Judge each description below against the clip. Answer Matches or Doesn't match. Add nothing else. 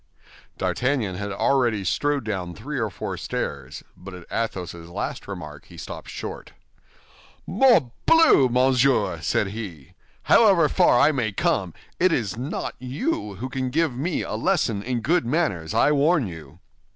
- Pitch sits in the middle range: Doesn't match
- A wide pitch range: Matches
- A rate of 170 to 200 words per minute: Doesn't match